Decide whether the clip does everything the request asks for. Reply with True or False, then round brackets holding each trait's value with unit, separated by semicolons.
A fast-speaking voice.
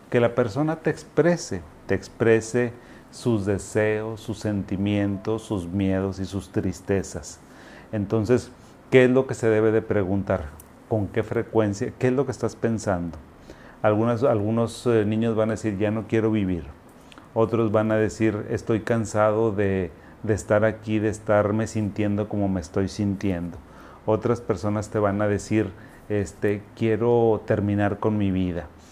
False (150 wpm)